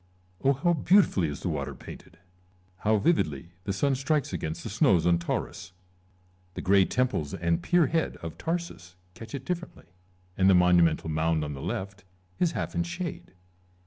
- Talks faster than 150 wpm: Yes, average, 175 wpm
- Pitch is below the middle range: Yes, very low, 95 Hz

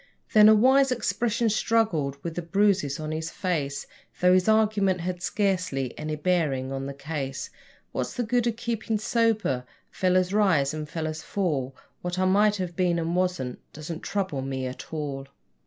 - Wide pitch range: Yes, wide, 5.9 semitones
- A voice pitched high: No, medium, 180 Hz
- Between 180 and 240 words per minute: No, average, 170 wpm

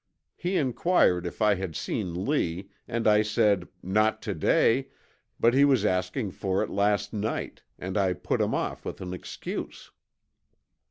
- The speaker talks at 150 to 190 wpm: Yes, average, 160 wpm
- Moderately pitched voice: No, low, 105 Hz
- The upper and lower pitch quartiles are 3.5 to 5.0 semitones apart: Yes, average, 3.8 semitones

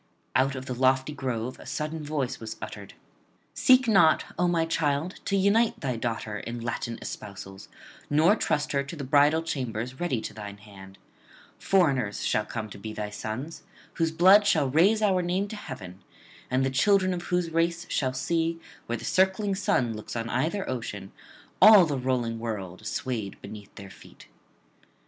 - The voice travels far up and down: Yes, wide, 7.0 semitones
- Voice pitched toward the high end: No, low, 135 Hz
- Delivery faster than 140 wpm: Yes, average, 170 wpm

